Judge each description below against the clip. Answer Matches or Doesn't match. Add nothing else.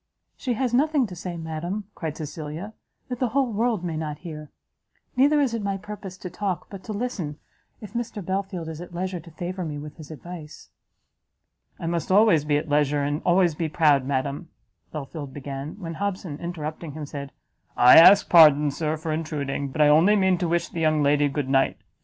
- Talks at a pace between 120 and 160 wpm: Doesn't match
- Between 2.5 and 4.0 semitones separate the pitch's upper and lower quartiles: Doesn't match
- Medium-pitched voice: Matches